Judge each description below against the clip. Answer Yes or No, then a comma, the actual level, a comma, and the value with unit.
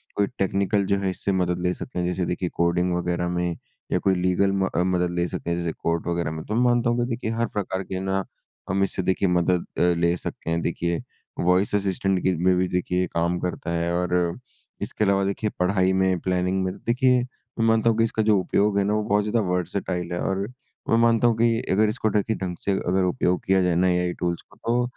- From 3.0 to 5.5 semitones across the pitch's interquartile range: No, narrow, 2.5 semitones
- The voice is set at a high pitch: No, very low, 95 Hz